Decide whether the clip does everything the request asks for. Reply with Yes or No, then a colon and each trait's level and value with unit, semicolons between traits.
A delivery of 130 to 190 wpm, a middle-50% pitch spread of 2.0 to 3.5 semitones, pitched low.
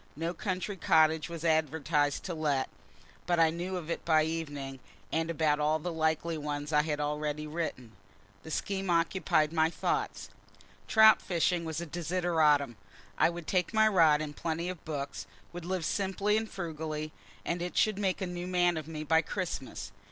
No: average, 175 wpm; narrow, 2.6 semitones; medium, 160 Hz